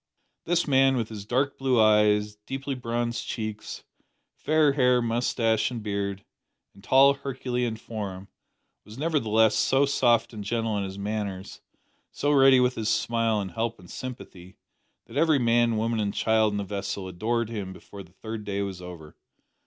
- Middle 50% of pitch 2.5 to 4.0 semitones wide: Yes, average, 3.6 semitones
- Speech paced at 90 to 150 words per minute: No, average, 165 wpm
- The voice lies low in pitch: Yes, low, 110 Hz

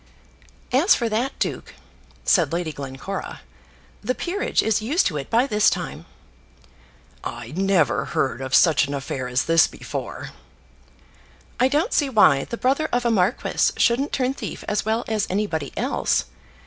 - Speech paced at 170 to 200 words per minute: No, average, 155 wpm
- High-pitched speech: Yes, high, 210 Hz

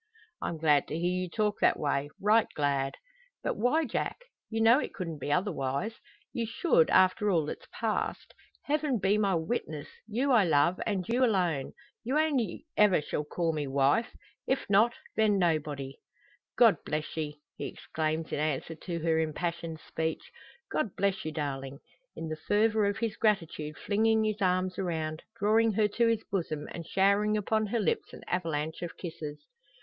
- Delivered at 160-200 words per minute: Yes, average, 170 wpm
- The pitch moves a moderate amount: No, wide, 5.7 semitones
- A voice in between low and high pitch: Yes, medium, 180 Hz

